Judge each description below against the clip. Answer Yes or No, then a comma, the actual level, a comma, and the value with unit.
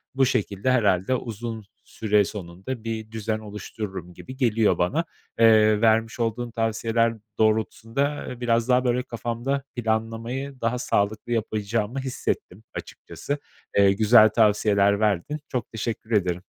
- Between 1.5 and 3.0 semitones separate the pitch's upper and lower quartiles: Yes, narrow, 2.4 semitones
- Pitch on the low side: Yes, low, 115 Hz